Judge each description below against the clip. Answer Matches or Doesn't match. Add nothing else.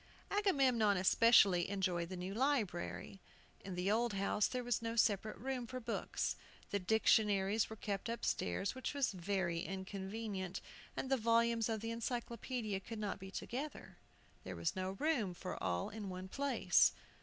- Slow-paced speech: Doesn't match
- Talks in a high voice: Matches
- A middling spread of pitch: Matches